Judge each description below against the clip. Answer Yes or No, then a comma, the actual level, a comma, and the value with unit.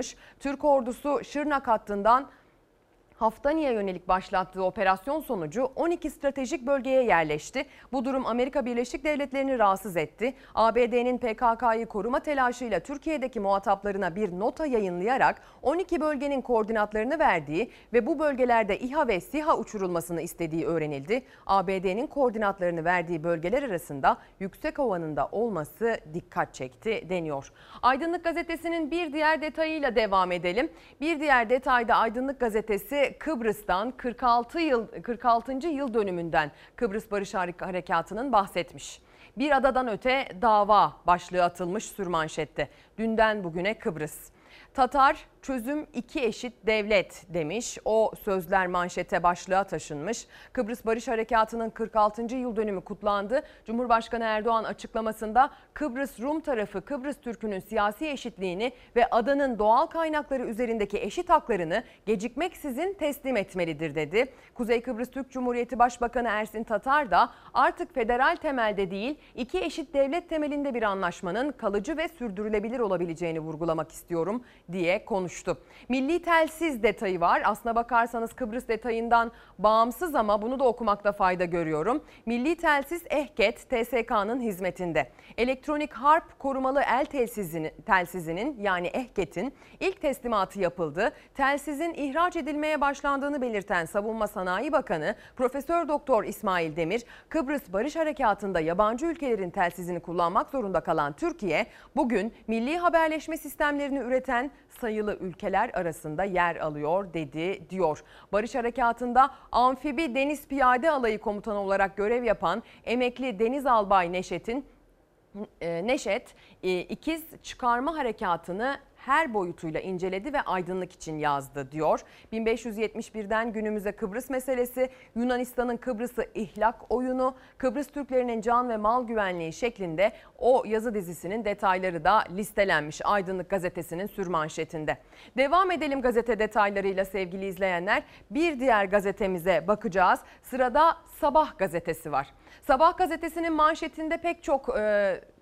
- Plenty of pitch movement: Yes, wide, 6.1 semitones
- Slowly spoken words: No, average, 120 wpm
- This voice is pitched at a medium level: No, high, 230 Hz